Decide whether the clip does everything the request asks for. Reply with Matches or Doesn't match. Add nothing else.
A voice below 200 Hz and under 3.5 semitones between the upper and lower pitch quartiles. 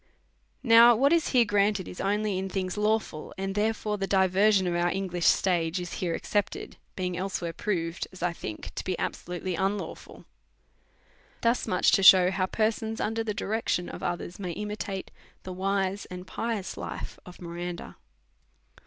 Matches